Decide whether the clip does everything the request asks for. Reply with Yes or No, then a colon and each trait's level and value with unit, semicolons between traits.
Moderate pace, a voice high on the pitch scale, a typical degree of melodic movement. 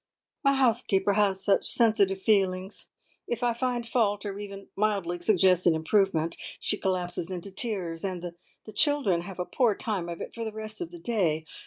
Yes: average, 180 wpm; high, 200 Hz; average, 3.5 semitones